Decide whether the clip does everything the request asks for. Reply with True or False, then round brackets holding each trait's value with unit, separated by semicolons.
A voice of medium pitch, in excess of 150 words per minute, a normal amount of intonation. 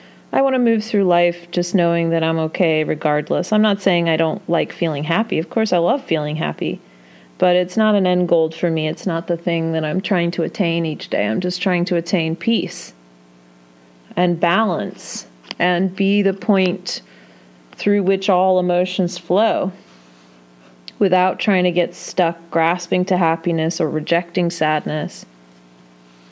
True (170 Hz; 165 wpm; 3.0 semitones)